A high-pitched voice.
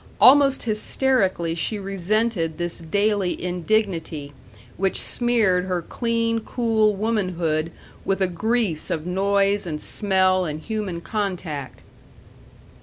Yes: high, 195 Hz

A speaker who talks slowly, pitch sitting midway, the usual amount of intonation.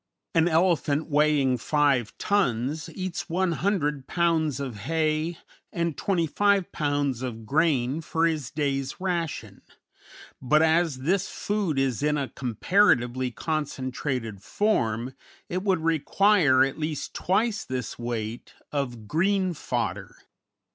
Yes: slow, 120 wpm; medium, 150 Hz; average, 4.8 semitones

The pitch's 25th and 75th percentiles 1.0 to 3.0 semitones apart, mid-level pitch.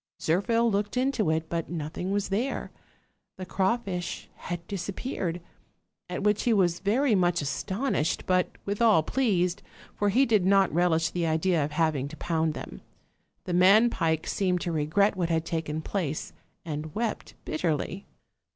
No: average, 4.0 semitones; medium, 180 Hz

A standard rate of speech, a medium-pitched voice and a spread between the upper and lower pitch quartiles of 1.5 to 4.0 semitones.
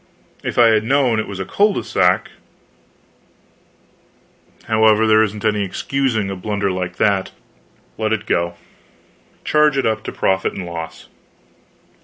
No: average, 145 wpm; low, 110 Hz; average, 2.8 semitones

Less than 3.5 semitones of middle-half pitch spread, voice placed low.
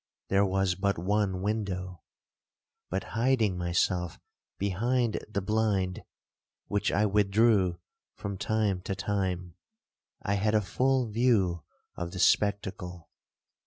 Yes: narrow, 2.6 semitones; low, 100 Hz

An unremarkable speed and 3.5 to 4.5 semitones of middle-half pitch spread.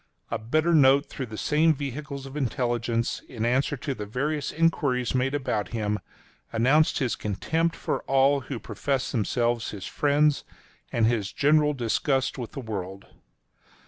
Yes: average, 150 wpm; average, 3.9 semitones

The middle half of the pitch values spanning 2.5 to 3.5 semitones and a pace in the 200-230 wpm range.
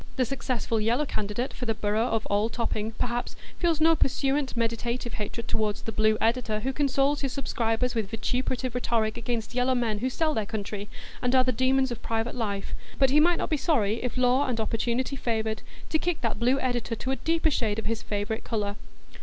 Yes: average, 3.0 semitones; fast, 205 wpm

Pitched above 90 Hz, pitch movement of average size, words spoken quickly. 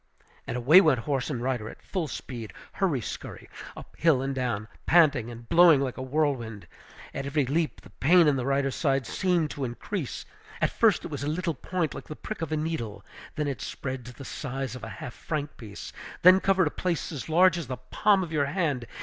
Yes: medium, 140 Hz; average, 4.6 semitones; fast, 220 wpm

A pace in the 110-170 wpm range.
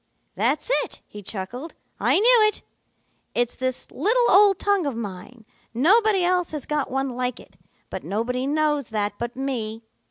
Yes: average, 160 wpm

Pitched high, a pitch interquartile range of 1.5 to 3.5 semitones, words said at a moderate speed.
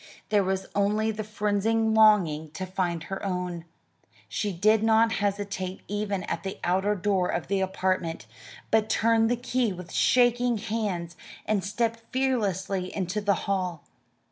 Yes: high, 200 Hz; average, 3.0 semitones; average, 145 wpm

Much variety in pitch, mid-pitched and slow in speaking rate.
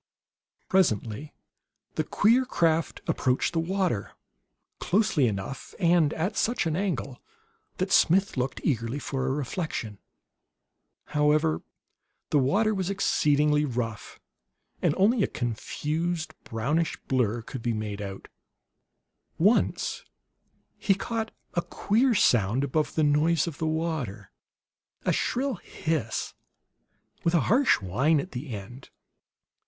Yes: wide, 6.5 semitones; medium, 155 Hz; slow, 120 wpm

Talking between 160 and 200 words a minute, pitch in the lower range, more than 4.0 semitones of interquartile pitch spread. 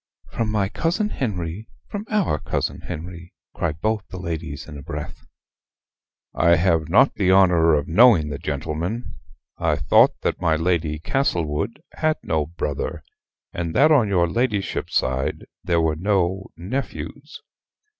No: average, 145 wpm; very low, 85 Hz; average, 5.1 semitones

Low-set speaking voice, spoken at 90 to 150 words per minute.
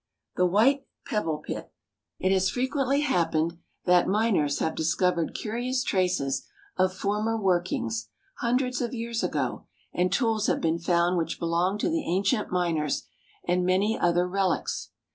No: medium, 185 Hz; average, 145 wpm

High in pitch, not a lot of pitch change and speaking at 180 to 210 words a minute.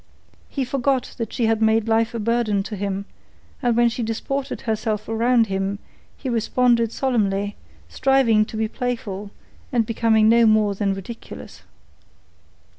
No: high, 225 Hz; narrow, 2.2 semitones; average, 145 wpm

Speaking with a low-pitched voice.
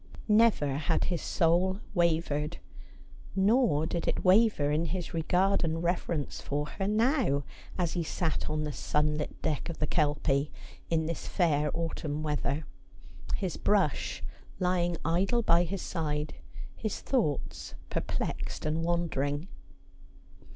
No: medium, 165 Hz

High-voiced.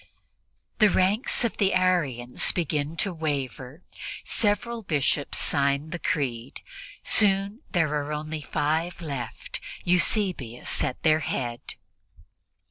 No: medium, 155 Hz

